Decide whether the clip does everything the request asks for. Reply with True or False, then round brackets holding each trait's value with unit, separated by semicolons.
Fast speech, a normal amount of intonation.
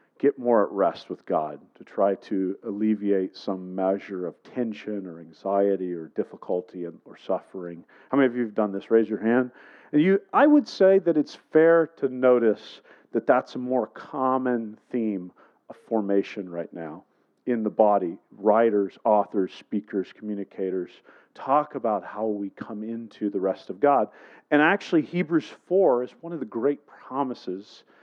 False (165 wpm; 4.6 semitones)